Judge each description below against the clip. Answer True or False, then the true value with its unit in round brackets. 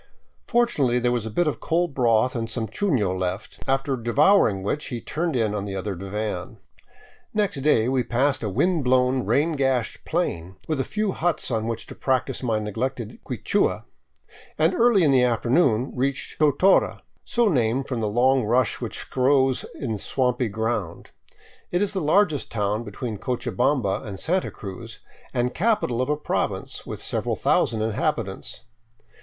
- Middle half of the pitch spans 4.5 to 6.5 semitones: True (4.9 semitones)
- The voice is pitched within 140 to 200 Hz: False (125 Hz)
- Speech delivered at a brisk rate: False (165 wpm)